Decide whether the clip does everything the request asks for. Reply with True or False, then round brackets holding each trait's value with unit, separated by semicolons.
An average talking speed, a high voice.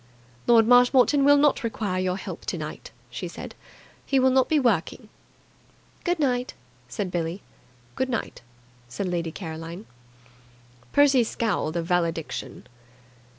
False (125 wpm; 225 Hz)